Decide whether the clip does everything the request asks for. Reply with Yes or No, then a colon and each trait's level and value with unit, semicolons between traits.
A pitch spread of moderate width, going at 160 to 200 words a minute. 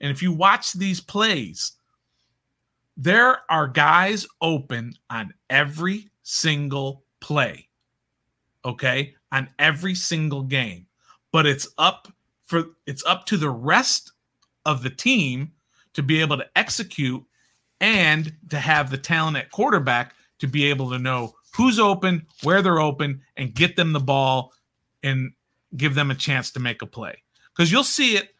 No: average, 4.9 semitones; average, 150 wpm